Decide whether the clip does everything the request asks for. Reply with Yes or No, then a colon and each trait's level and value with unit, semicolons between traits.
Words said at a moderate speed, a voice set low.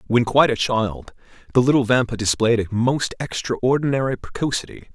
Yes: average, 145 wpm; low, 120 Hz